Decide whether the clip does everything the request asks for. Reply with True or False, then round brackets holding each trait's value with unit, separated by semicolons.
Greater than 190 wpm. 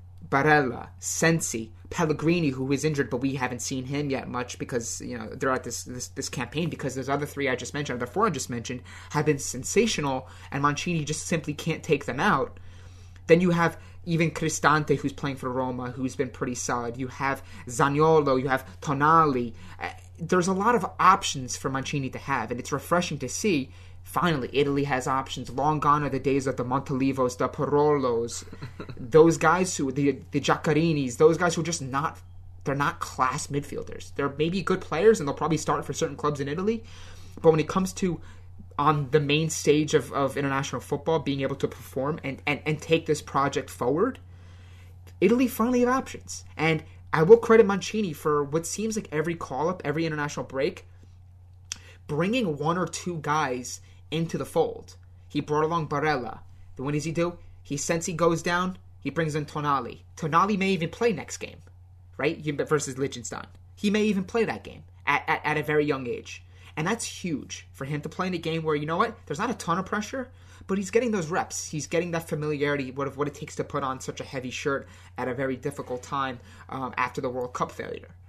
True (200 wpm)